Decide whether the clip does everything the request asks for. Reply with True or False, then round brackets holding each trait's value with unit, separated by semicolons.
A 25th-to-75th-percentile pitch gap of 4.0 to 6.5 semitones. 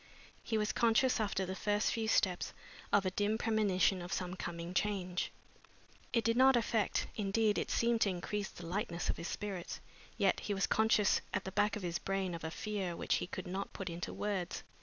False (2.9 semitones)